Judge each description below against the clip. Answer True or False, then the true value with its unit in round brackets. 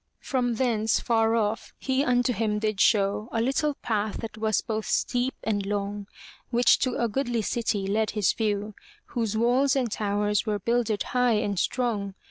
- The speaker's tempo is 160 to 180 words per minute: True (170 wpm)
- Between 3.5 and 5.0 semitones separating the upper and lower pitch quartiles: False (2.7 semitones)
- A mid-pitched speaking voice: False (220 Hz)